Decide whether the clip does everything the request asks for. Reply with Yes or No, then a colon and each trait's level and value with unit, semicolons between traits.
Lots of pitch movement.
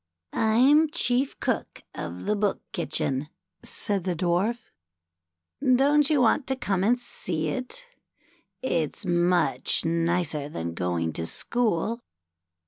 Yes: wide, 7.9 semitones